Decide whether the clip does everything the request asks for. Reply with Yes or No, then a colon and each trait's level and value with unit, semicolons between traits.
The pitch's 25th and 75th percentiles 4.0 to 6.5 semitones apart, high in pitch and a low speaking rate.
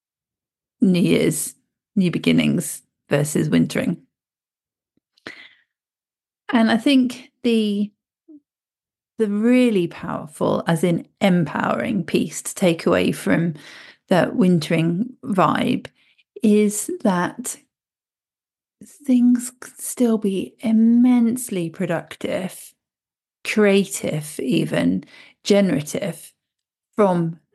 Yes: wide, 5.4 semitones; high, 210 Hz; slow, 75 wpm